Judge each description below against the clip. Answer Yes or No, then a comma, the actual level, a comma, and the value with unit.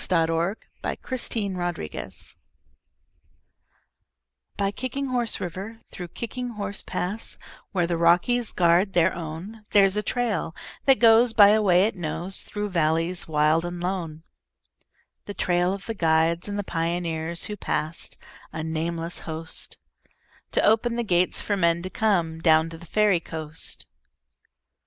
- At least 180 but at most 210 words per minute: No, average, 140 wpm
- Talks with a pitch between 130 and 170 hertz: No, medium, 180 Hz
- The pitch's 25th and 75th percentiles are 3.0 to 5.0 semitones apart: Yes, average, 4.1 semitones